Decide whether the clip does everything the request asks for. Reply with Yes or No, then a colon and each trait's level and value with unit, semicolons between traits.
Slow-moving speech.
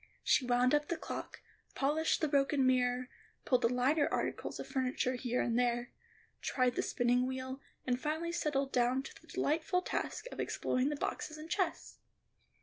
No: average, 175 wpm